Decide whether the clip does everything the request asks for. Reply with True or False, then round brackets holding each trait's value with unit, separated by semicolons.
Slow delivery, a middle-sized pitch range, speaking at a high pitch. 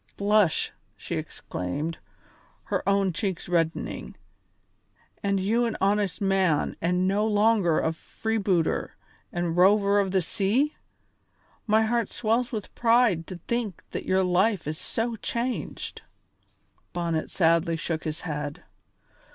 True (125 wpm; 4.5 semitones; 195 Hz)